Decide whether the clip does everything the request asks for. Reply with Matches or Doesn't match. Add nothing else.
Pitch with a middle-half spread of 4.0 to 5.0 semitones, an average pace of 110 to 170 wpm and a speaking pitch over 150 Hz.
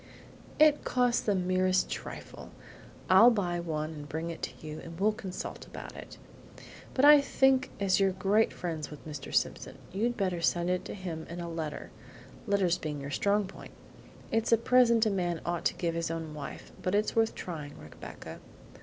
Doesn't match